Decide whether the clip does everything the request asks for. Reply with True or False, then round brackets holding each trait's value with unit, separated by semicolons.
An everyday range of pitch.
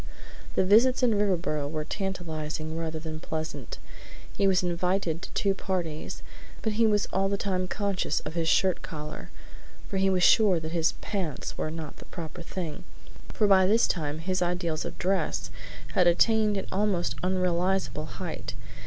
True (3.5 semitones)